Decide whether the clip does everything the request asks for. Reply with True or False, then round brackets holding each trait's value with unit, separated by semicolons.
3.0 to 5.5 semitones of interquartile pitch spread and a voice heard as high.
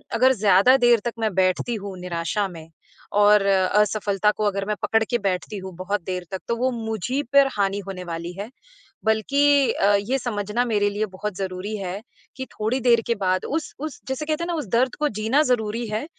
True (3.9 semitones; 210 Hz)